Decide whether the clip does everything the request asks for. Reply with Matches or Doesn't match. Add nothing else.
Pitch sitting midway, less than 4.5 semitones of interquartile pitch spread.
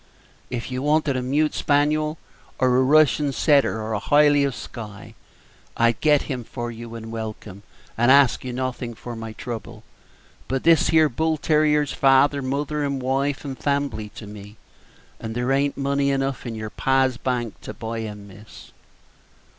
Doesn't match